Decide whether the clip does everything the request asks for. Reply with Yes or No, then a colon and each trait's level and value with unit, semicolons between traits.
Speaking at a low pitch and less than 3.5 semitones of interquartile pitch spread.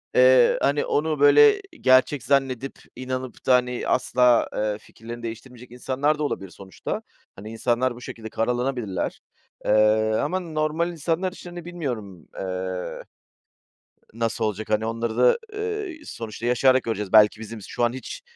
No: low, 125 Hz; average, 4.5 semitones